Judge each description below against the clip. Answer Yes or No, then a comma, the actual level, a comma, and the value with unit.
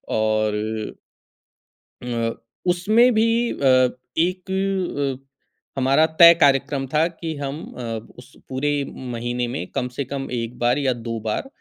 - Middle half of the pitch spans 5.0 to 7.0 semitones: Yes, wide, 5.6 semitones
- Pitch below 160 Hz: Yes, low, 135 Hz